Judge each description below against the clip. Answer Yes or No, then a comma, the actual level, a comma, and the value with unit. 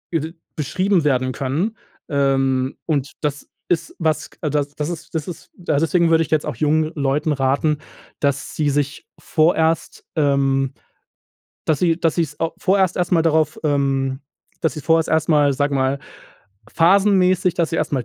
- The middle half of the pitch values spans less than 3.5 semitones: Yes, average, 2.8 semitones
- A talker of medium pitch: Yes, medium, 155 Hz